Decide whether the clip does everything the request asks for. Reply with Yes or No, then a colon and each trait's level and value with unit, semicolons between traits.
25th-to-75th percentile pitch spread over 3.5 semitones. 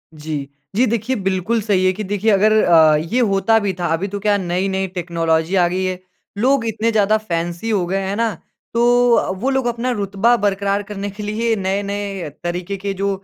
No: average, 3.0 semitones